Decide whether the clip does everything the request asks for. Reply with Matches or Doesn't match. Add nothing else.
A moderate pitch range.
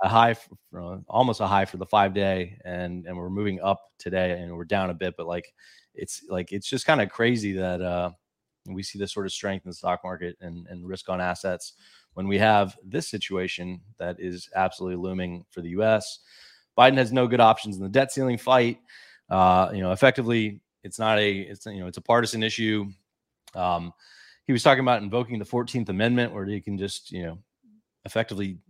Matches